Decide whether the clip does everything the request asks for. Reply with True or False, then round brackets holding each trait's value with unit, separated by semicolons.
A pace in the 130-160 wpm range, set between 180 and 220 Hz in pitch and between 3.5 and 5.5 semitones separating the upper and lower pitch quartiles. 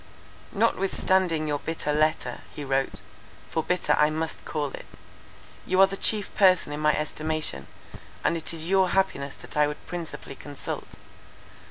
False (155 wpm; 155 Hz; 3.8 semitones)